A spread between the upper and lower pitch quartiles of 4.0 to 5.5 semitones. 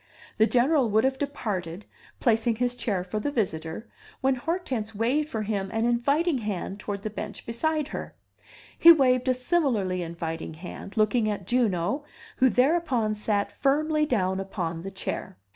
Yes: average, 5.1 semitones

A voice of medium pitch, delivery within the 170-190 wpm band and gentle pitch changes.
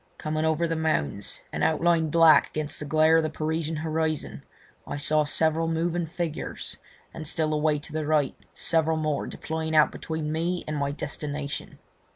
Yes: medium, 155 Hz; average, 175 wpm; narrow, 1.1 semitones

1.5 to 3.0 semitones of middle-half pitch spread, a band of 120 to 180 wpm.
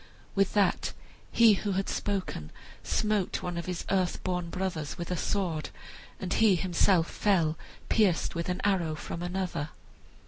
Yes: narrow, 2.5 semitones; average, 150 wpm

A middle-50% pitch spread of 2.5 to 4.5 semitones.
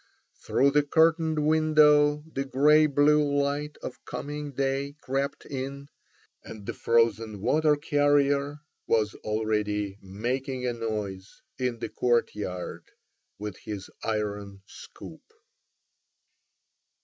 No: average, 5.3 semitones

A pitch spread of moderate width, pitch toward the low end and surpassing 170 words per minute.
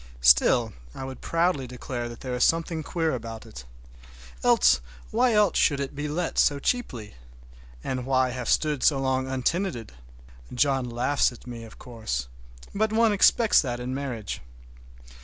No: average, 4.8 semitones; low, 130 Hz; average, 155 wpm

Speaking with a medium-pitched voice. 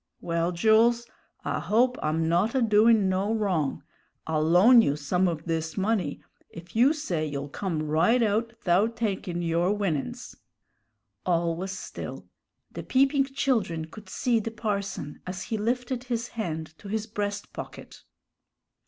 No: high, 200 Hz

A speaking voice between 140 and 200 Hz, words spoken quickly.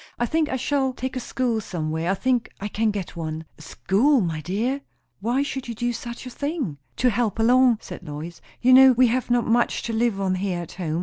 No: high, 230 Hz; fast, 230 wpm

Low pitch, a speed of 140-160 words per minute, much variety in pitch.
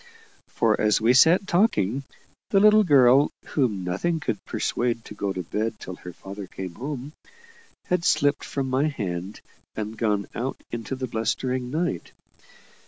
Yes: low, 125 Hz; average, 155 wpm; wide, 5.7 semitones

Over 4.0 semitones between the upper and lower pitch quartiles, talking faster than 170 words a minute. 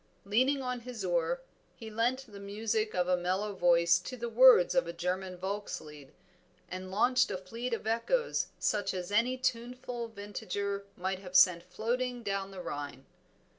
No: average, 4.9 semitones; average, 165 wpm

